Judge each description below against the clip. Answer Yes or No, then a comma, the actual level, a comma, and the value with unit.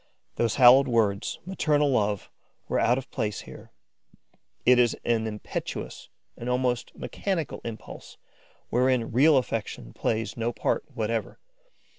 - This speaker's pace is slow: Yes, slow, 125 wpm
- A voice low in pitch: Yes, low, 120 Hz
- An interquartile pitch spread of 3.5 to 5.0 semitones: No, average, 2.8 semitones